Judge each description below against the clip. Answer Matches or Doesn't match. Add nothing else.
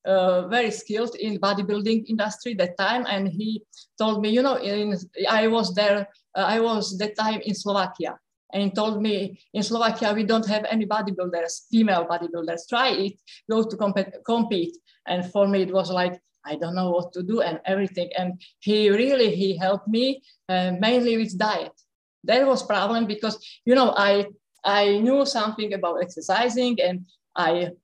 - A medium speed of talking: Matches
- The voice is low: Doesn't match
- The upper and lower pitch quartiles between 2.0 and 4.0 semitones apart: Matches